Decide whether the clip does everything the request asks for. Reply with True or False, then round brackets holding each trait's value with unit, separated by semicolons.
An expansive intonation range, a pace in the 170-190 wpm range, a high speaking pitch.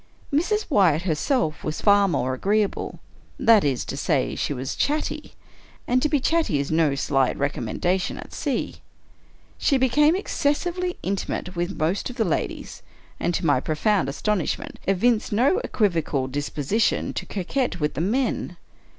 False (9.0 semitones; 150 wpm; 195 Hz)